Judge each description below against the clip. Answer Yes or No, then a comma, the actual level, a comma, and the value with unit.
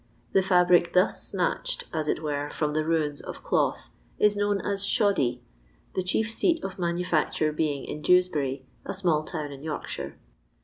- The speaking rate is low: No, average, 165 wpm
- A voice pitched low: No, medium, 170 Hz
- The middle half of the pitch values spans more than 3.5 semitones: Yes, average, 4.1 semitones